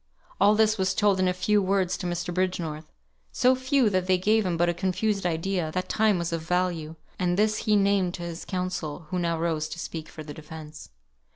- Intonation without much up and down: No, average, 3.0 semitones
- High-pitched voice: No, medium, 180 Hz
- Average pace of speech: No, fast, 215 wpm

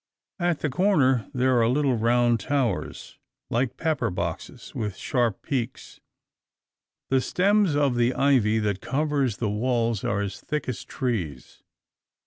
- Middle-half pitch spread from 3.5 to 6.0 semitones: Yes, average, 4.3 semitones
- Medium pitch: No, low, 125 Hz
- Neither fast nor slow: No, slow, 130 wpm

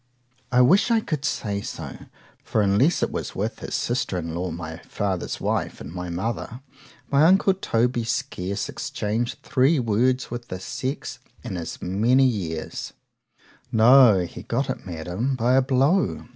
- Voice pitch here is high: No, low, 120 Hz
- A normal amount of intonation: No, wide, 6.1 semitones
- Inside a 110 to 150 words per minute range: Yes, average, 145 wpm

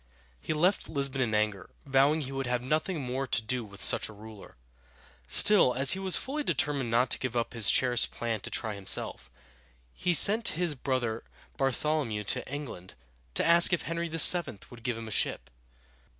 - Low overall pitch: Yes, low, 130 Hz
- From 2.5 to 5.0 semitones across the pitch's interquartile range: No, wide, 5.4 semitones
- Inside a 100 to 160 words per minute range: No, average, 195 wpm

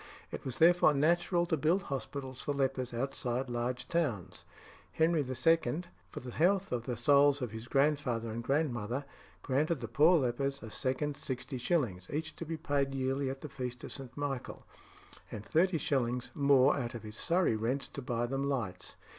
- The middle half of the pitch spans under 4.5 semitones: Yes, average, 3.7 semitones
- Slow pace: No, average, 175 wpm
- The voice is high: No, low, 135 Hz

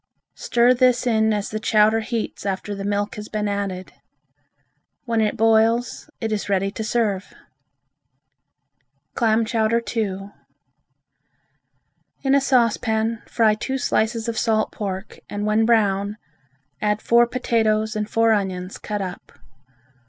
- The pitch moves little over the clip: Yes, narrow, 1.9 semitones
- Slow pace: Yes, slow, 130 wpm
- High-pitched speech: Yes, high, 220 Hz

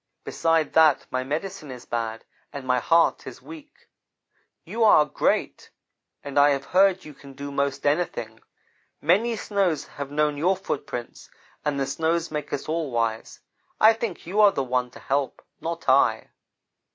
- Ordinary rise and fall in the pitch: Yes, average, 4.7 semitones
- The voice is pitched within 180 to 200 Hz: No, medium, 150 Hz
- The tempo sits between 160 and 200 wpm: Yes, average, 165 wpm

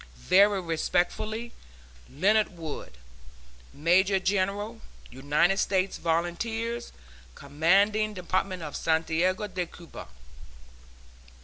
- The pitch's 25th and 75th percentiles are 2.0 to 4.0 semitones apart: Yes, average, 3.7 semitones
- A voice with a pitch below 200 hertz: Yes, medium, 185 Hz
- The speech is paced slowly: Yes, slow, 80 wpm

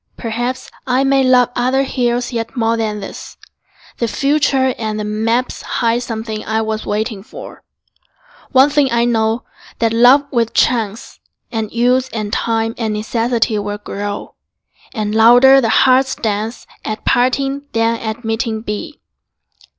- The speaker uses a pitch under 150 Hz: No, high, 230 Hz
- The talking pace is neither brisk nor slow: Yes, average, 145 wpm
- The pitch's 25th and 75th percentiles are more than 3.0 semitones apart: No, narrow, 2.6 semitones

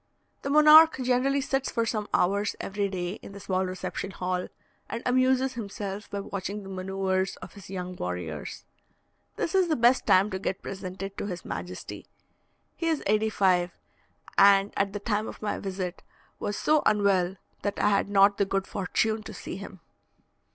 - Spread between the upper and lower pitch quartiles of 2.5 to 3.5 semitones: Yes, average, 2.9 semitones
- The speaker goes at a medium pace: Yes, average, 175 wpm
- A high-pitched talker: Yes, high, 200 Hz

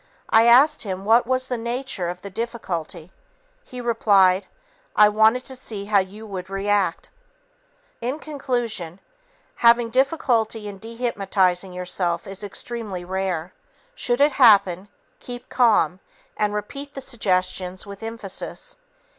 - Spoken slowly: Yes, slow, 130 wpm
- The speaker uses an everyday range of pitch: Yes, average, 4.2 semitones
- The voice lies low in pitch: No, high, 210 Hz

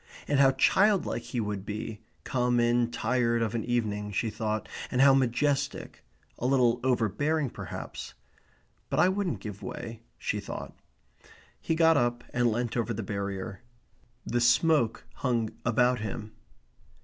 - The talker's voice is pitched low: Yes, low, 120 Hz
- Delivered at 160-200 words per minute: No, average, 145 wpm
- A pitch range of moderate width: Yes, average, 3.2 semitones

